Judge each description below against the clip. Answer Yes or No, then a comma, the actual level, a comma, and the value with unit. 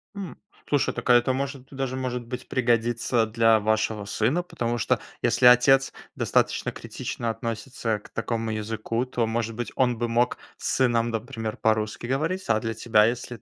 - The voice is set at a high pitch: No, low, 120 Hz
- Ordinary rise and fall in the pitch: No, narrow, 2.1 semitones